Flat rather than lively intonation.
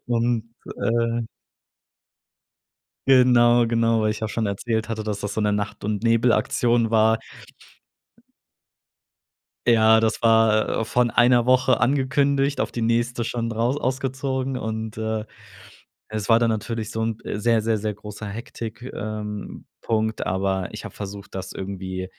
Yes: narrow, 1.8 semitones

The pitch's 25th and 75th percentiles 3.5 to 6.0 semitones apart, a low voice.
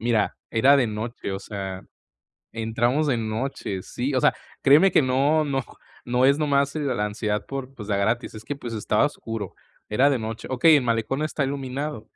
Yes: average, 4.2 semitones; low, 125 Hz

